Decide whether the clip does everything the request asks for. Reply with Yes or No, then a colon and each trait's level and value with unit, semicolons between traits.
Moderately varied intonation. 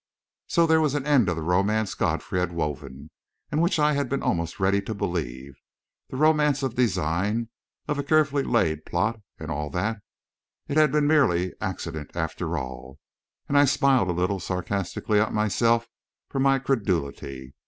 No: wide, 8.3 semitones